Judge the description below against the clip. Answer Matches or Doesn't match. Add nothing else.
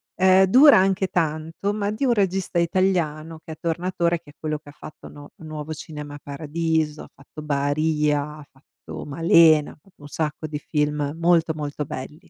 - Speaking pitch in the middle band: Matches